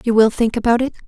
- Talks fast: Yes, fast, 280 wpm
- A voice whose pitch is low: No, high, 230 Hz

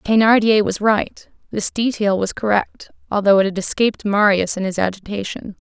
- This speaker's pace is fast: No, average, 160 wpm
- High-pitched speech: Yes, high, 205 Hz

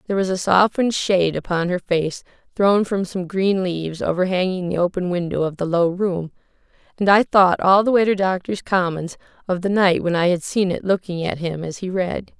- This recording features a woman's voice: Yes, female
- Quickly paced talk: Yes, fast, 215 wpm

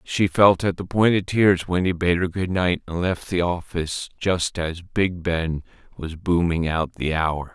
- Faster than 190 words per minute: Yes, fast, 205 wpm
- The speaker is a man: Yes, male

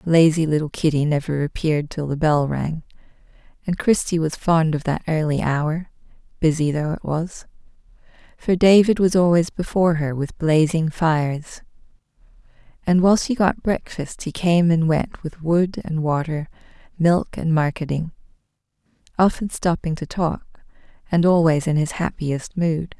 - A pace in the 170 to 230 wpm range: No, average, 145 wpm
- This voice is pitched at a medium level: Yes, medium, 160 Hz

